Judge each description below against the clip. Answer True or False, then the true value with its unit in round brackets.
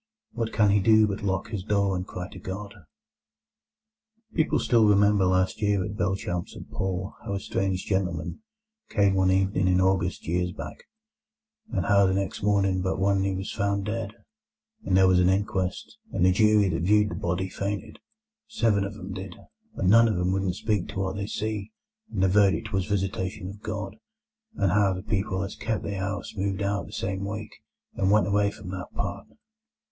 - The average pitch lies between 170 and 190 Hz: False (100 Hz)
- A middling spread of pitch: False (1.6 semitones)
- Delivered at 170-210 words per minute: True (195 wpm)